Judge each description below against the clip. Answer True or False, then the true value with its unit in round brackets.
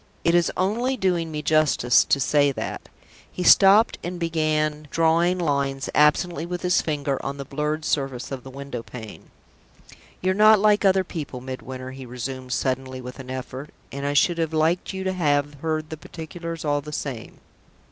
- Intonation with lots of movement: False (4.2 semitones)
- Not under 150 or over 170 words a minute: False (180 wpm)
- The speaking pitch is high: False (150 Hz)